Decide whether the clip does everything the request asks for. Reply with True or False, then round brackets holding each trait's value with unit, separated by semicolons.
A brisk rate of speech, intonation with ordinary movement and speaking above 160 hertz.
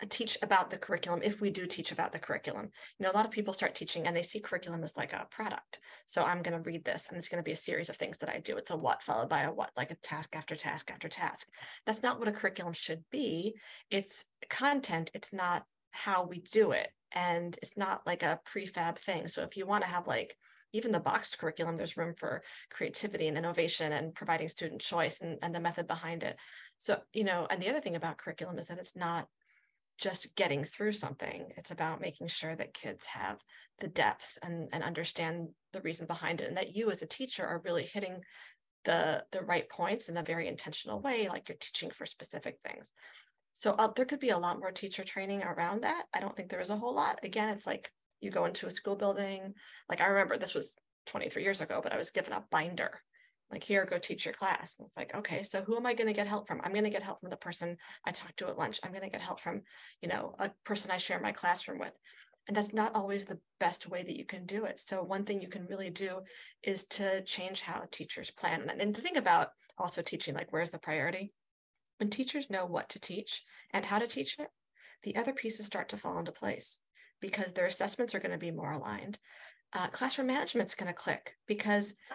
True (235 wpm; 3.5 semitones; 190 Hz)